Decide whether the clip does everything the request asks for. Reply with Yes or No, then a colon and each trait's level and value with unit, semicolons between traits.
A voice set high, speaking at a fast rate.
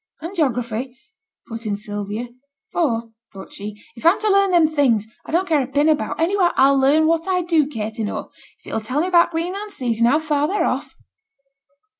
Yes: very high, 290 Hz; fast, 215 wpm